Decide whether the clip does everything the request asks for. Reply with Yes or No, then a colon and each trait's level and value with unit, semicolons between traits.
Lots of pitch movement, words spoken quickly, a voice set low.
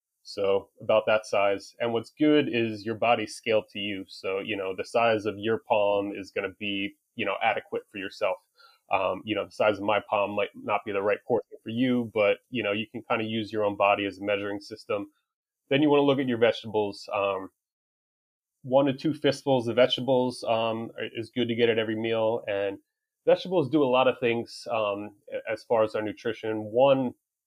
Yes: wide, 5.8 semitones; fast, 215 wpm; low, 115 Hz